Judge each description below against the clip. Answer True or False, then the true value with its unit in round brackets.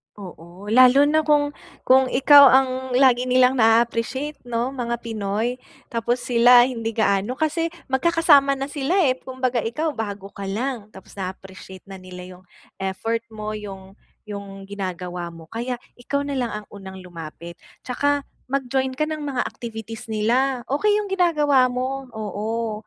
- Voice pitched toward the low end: False (235 Hz)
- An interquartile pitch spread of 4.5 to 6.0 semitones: True (4.8 semitones)